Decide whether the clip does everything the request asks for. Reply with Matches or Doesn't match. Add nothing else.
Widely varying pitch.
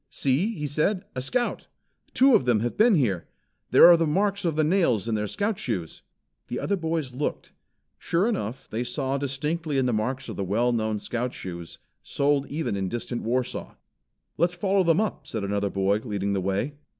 Matches